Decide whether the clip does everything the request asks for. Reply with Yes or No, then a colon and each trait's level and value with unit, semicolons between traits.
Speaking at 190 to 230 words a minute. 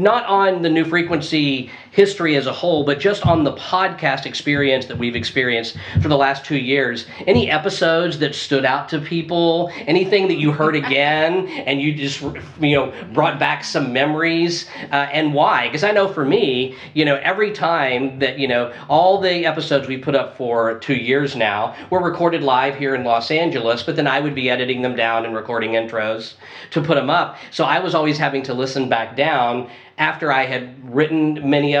Yes: average, 200 wpm